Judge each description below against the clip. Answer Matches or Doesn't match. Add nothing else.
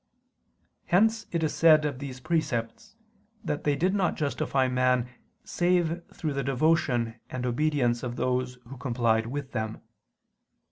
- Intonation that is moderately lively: Matches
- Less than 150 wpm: Matches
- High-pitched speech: Doesn't match